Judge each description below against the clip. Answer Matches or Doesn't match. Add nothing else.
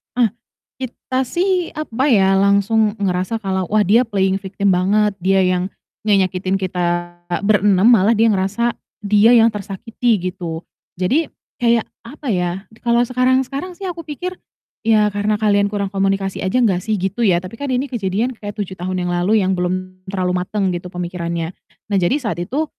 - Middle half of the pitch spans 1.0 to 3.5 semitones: Doesn't match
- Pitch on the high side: Matches